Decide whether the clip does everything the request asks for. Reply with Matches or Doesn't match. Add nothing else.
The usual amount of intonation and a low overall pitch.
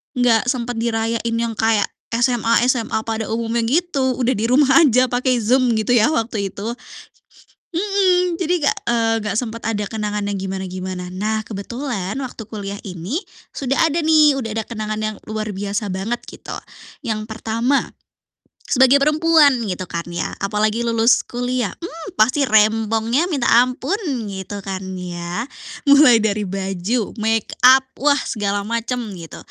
Doesn't match